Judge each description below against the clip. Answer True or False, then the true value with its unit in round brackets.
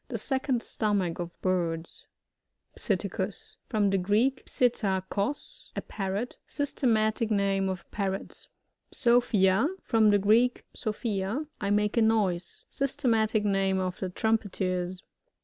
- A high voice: True (205 Hz)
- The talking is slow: True (130 wpm)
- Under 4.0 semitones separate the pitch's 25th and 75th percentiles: True (3.2 semitones)